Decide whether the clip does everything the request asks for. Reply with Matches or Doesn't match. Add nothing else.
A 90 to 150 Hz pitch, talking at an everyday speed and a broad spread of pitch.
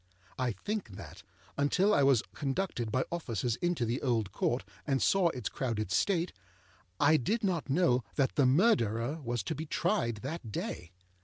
Matches